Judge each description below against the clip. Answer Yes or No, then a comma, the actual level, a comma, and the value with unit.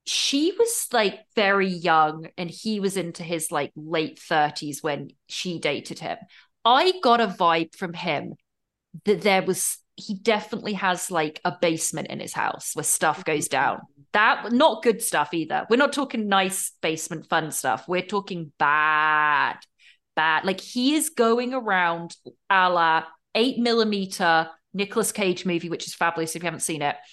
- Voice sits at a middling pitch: Yes, medium, 180 Hz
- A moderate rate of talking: Yes, average, 165 wpm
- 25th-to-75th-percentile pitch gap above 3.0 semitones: Yes, average, 4.7 semitones